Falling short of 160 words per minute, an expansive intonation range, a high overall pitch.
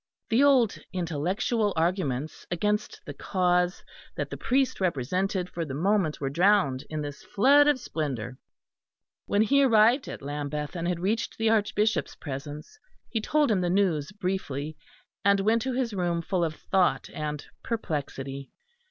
No: average, 150 wpm; wide, 6.2 semitones; medium, 180 Hz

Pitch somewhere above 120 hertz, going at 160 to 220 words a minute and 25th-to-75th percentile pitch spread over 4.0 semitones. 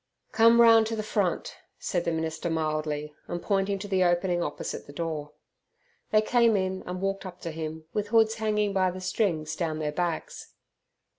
Yes: medium, 185 Hz; average, 180 wpm; average, 4.6 semitones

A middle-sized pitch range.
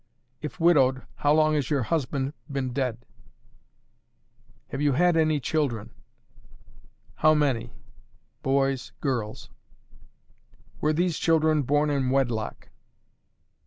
Yes: average, 3.0 semitones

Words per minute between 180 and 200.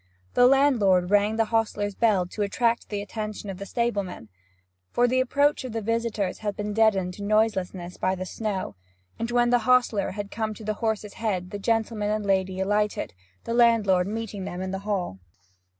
Yes: average, 190 wpm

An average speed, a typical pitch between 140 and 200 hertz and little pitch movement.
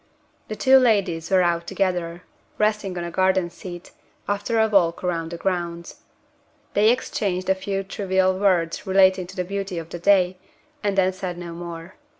Yes: average, 170 wpm; medium, 185 Hz; narrow, 2.3 semitones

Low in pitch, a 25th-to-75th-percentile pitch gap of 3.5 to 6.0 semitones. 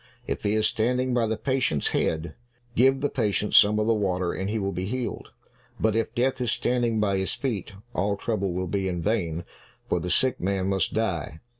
Yes: low, 105 Hz; average, 3.8 semitones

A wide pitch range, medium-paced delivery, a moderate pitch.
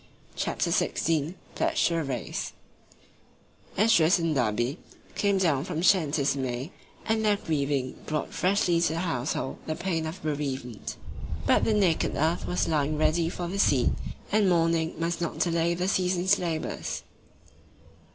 No: average, 3.5 semitones; average, 150 wpm; medium, 165 Hz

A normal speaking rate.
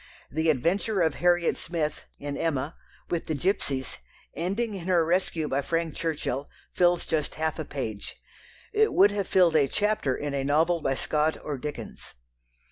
Yes: average, 165 wpm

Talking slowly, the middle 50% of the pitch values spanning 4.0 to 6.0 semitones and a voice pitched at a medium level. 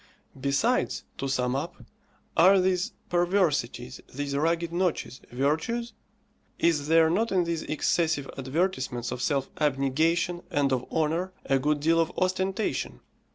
Yes: slow, 130 wpm; average, 4.5 semitones; medium, 160 Hz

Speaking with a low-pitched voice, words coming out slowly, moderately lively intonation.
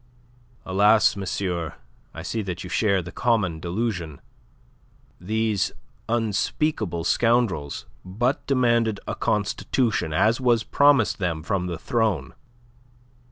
Yes: low, 105 Hz; slow, 110 wpm; average, 4.7 semitones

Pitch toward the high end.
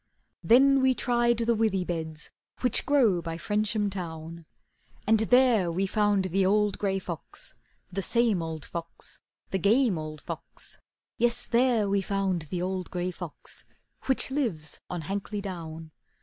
Yes: high, 195 Hz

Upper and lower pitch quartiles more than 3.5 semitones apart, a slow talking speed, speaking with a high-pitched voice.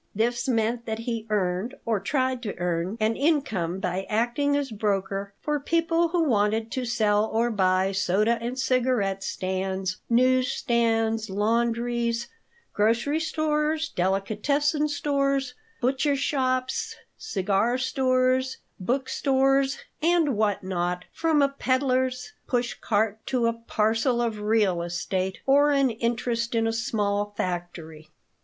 Yes: average, 4.4 semitones; slow, 130 wpm; high, 230 Hz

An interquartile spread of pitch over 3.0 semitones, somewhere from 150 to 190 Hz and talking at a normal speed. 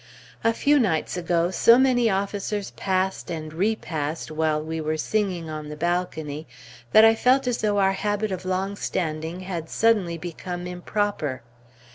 Yes: average, 4.4 semitones; medium, 185 Hz; average, 155 wpm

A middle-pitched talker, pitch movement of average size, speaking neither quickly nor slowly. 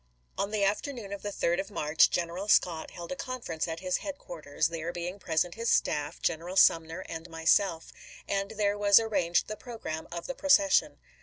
Yes: medium, 180 Hz; average, 3.9 semitones; average, 185 wpm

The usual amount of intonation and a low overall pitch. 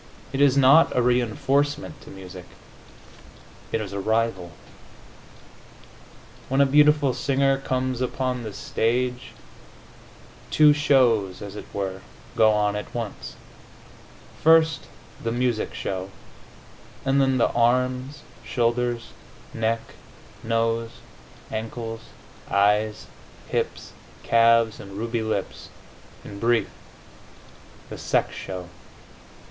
Yes: average, 3.4 semitones; low, 115 Hz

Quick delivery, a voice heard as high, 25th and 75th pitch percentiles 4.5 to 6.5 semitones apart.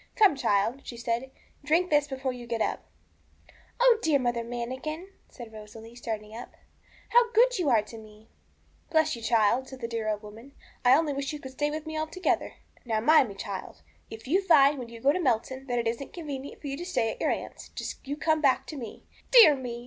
Yes: fast, 220 wpm; very high, 260 Hz; average, 4.9 semitones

